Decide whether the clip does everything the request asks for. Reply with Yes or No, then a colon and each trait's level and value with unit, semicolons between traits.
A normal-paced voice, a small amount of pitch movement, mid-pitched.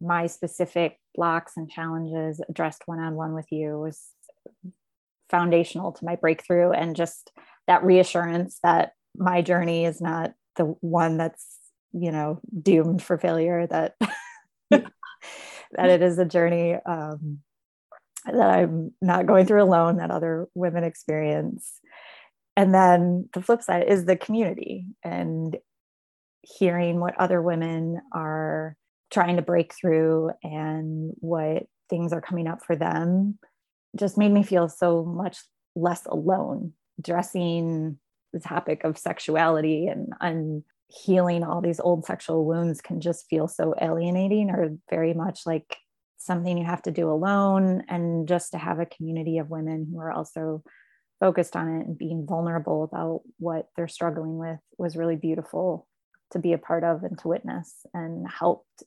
Yes: average, 150 wpm; narrow, 1.7 semitones; medium, 170 Hz